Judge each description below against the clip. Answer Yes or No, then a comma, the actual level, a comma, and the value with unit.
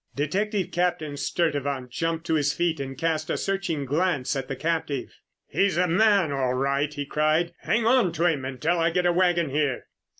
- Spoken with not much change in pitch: No, average, 3.9 semitones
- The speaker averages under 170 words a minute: No, average, 190 wpm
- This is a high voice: No, medium, 160 Hz